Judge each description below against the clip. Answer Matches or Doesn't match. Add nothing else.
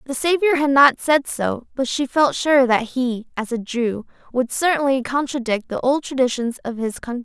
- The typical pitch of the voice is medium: Doesn't match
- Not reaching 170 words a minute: Doesn't match